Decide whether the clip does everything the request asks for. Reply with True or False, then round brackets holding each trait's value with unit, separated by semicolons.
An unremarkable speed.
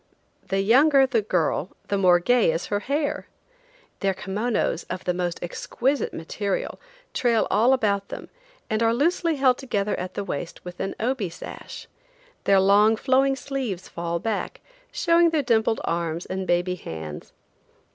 True (155 wpm)